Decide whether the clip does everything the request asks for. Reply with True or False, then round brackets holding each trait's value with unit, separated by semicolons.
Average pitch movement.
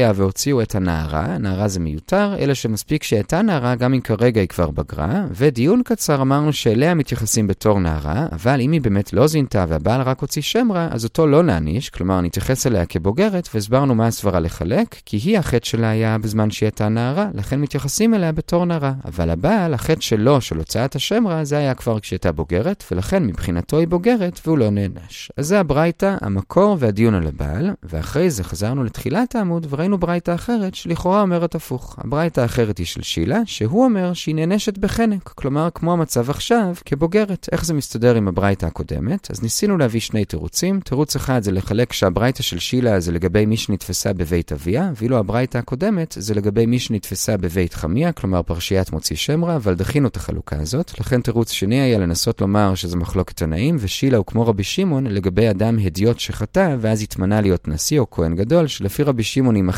False (8.3 semitones)